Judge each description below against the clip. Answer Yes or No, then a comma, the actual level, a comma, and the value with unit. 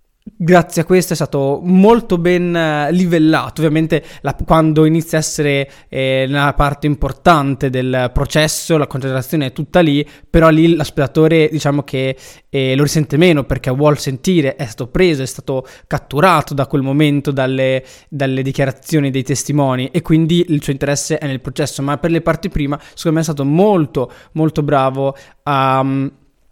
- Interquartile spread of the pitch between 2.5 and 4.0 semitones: Yes, average, 2.9 semitones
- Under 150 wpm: No, average, 165 wpm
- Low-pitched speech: No, medium, 145 Hz